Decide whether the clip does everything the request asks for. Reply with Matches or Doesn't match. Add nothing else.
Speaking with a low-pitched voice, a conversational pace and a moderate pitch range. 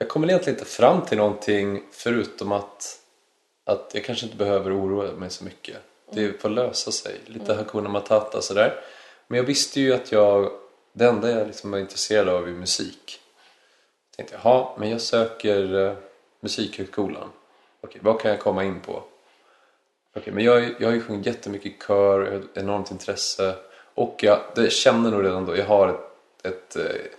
Matches